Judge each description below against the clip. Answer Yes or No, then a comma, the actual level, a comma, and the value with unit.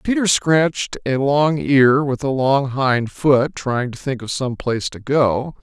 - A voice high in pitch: No, low, 135 Hz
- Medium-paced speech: Yes, average, 190 wpm